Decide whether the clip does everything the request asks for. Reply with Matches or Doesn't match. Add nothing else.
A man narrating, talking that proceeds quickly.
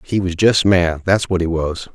Matches